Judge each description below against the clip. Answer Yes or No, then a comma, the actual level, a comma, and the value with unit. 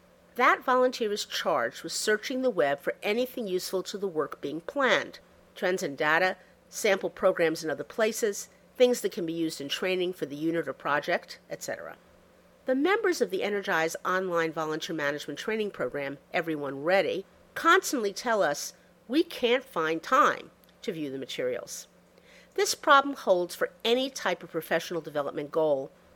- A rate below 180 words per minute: Yes, average, 160 wpm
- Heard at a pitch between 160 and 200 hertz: Yes, medium, 185 Hz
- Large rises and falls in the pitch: Yes, wide, 7.1 semitones